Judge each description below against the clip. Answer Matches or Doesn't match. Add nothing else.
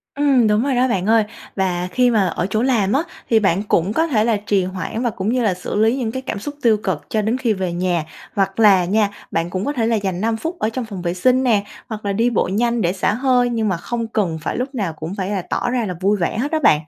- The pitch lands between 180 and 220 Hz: Matches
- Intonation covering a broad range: Doesn't match